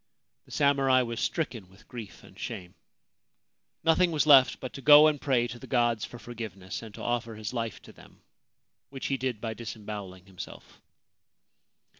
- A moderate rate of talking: Yes, average, 170 wpm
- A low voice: Yes, low, 120 Hz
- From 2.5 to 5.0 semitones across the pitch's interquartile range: Yes, average, 4.0 semitones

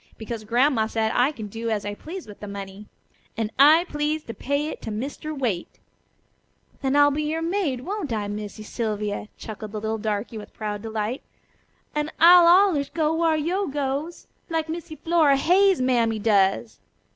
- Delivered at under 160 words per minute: No, average, 175 wpm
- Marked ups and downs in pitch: Yes, wide, 6.4 semitones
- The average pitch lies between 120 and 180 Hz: No, very high, 260 Hz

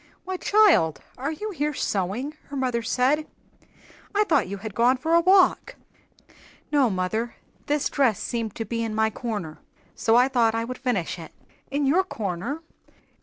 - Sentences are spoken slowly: No, average, 170 wpm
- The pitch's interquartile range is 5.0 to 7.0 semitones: Yes, average, 5.3 semitones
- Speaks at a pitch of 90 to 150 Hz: No, very high, 250 Hz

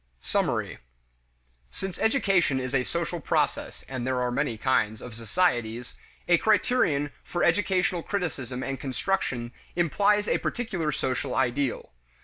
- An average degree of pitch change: No, wide, 6.9 semitones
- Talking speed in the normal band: No, slow, 125 wpm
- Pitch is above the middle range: No, medium, 140 Hz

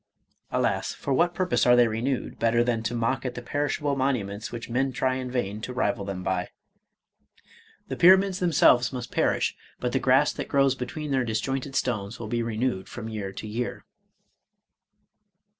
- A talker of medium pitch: No, low, 125 Hz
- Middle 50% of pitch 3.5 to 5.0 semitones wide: No, average, 3.1 semitones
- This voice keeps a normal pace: Yes, average, 185 wpm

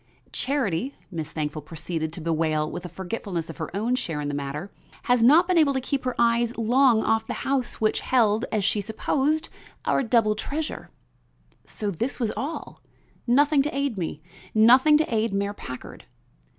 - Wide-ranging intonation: Yes, wide, 7.6 semitones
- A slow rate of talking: No, average, 175 wpm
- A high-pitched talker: Yes, high, 220 Hz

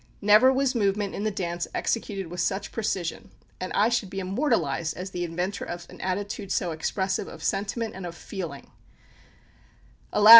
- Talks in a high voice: Yes, high, 195 Hz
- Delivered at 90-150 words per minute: No, average, 165 wpm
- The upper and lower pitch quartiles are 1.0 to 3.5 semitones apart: Yes, average, 3.0 semitones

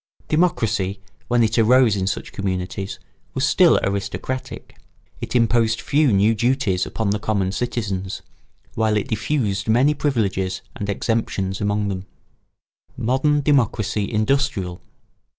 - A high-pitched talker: No, low, 110 Hz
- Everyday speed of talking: No, slow, 125 wpm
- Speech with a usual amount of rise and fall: Yes, average, 3.9 semitones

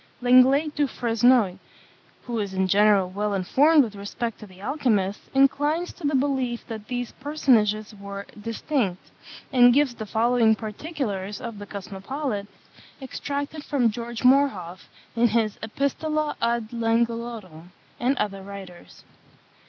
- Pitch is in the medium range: No, high, 230 Hz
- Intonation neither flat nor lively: Yes, average, 4.7 semitones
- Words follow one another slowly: Yes, slow, 130 wpm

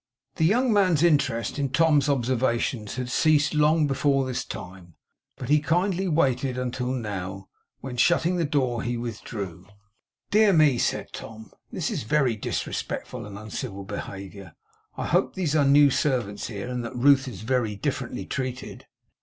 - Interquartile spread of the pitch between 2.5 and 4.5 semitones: No, average, 5.2 semitones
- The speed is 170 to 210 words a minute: No, average, 155 wpm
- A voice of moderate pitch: No, low, 130 Hz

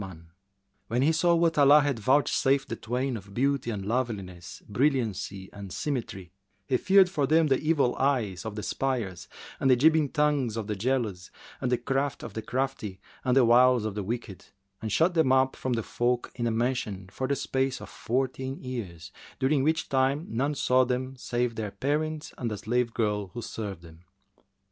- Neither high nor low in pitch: No, low, 125 Hz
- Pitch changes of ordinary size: Yes, average, 4.2 semitones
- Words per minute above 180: Yes, average, 190 wpm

